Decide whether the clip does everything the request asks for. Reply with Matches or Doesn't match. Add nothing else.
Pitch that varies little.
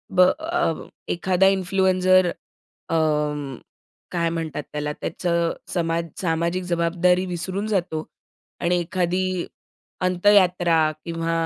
Matches